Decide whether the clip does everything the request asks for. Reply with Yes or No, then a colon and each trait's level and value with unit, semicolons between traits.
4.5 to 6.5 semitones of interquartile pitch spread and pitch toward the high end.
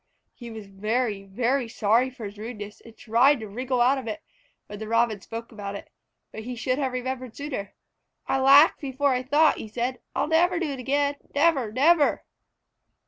No: average, 3.9 semitones; very high, 250 Hz